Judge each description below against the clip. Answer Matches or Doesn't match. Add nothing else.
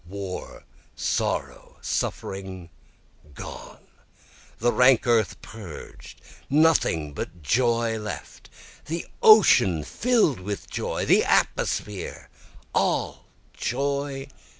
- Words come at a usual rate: Doesn't match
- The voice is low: Matches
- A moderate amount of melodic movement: Doesn't match